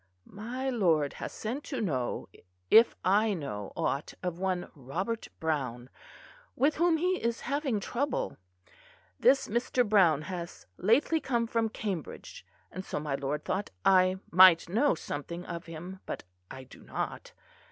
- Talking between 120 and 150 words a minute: Yes, average, 145 wpm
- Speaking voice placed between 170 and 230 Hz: Yes, high, 190 Hz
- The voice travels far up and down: Yes, wide, 6.6 semitones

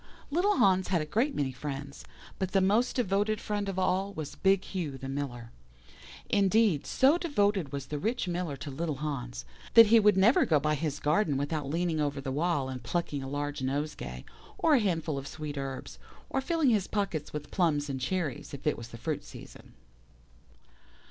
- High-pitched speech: No, medium, 160 Hz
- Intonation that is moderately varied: No, wide, 6.1 semitones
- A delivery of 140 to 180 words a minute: No, average, 190 wpm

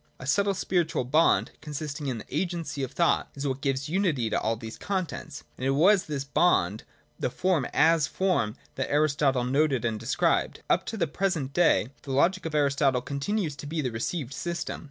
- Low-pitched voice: No, medium, 145 Hz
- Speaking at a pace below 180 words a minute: No, average, 195 wpm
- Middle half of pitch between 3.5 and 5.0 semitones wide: Yes, average, 4.5 semitones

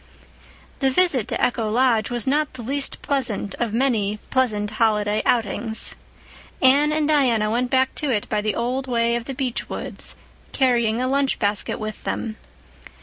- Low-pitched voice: No, high, 240 Hz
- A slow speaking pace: No, average, 165 wpm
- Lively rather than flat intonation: No, average, 3.5 semitones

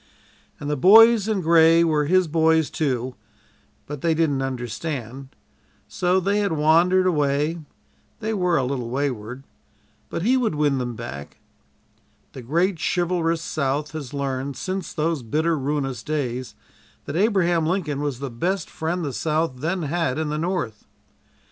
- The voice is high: No, medium, 155 Hz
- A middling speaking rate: Yes, average, 150 wpm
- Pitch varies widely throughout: No, average, 4.3 semitones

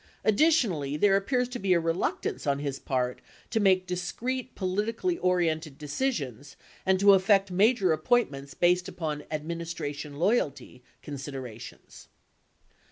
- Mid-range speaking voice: Yes, medium, 180 Hz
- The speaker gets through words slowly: Yes, slow, 130 wpm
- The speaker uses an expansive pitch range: Yes, wide, 5.8 semitones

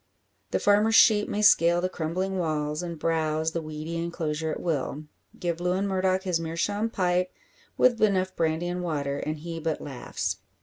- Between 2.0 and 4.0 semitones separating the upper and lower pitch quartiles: Yes, average, 3.0 semitones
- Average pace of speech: Yes, average, 170 wpm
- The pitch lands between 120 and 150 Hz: No, medium, 170 Hz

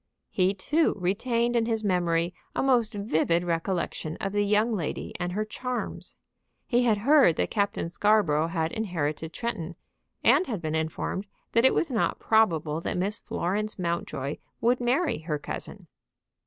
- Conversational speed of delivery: Yes, average, 155 wpm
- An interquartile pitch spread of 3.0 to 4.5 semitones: No, wide, 5.4 semitones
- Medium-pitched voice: No, high, 200 Hz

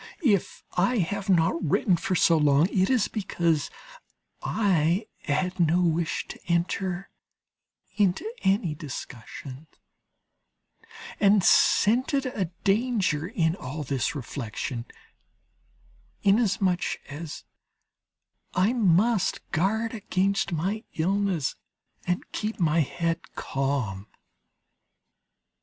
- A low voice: No, medium, 180 Hz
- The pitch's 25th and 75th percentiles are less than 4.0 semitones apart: No, average, 4.3 semitones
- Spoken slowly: Yes, slow, 95 wpm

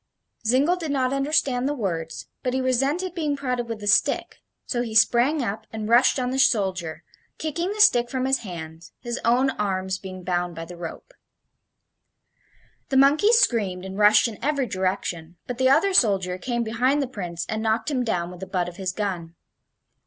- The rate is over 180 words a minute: Yes, average, 190 wpm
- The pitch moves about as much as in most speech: No, wide, 6.2 semitones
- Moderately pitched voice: No, high, 230 Hz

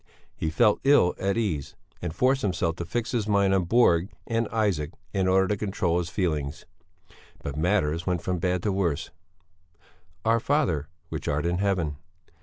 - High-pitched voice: No, very low, 95 Hz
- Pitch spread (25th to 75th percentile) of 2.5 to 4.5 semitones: Yes, average, 4.2 semitones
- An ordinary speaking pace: Yes, average, 170 wpm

